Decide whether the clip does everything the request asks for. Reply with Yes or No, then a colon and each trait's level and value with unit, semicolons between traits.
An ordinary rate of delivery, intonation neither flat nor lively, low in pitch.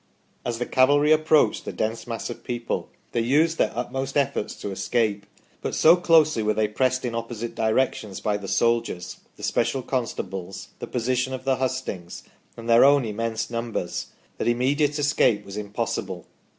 Yes: average, 170 wpm; average, 3.5 semitones; low, 120 Hz